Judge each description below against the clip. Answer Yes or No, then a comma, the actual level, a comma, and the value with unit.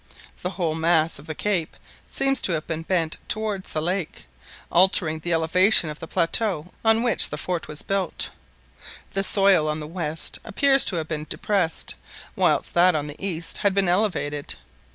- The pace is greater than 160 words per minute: Yes, average, 175 wpm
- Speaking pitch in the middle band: Yes, medium, 175 Hz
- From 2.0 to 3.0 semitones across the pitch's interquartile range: No, average, 3.8 semitones